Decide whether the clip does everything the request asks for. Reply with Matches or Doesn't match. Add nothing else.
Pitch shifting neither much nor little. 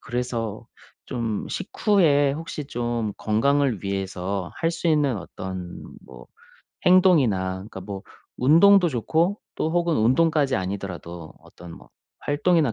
Doesn't match